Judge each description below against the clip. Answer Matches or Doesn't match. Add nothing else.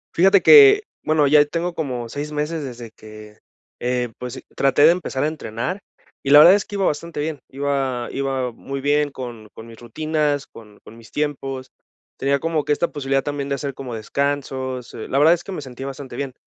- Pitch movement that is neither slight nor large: Matches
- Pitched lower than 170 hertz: Matches